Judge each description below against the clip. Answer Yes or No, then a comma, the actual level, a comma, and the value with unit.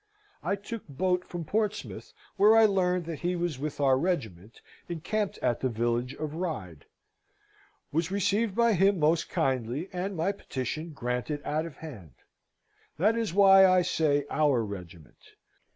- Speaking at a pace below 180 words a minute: Yes, average, 150 wpm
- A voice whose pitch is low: No, medium, 165 Hz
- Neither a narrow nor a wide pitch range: No, wide, 6.4 semitones